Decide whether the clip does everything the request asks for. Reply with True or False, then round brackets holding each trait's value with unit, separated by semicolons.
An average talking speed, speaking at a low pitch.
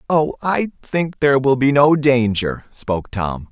True (170 wpm; 130 Hz)